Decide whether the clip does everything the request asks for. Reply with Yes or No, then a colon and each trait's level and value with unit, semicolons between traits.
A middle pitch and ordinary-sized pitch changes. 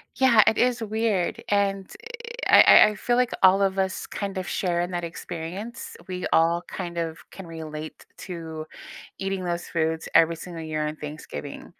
Yes: medium, 180 Hz; average, 3.3 semitones